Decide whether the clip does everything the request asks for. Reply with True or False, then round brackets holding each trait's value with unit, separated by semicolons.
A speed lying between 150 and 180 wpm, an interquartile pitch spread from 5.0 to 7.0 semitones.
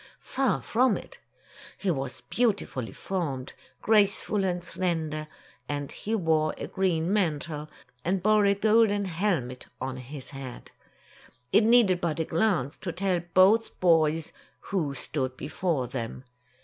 False (135 wpm; 5.5 semitones)